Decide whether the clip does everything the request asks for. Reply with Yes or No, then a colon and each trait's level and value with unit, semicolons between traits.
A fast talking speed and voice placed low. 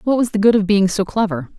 No: fast, 300 wpm; high, 205 Hz